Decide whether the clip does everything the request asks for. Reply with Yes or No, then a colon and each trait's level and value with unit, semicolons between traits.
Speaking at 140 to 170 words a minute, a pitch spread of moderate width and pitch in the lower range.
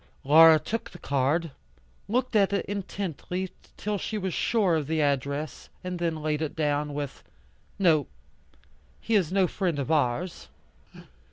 No: average, 150 wpm; average, 4.5 semitones; medium, 165 Hz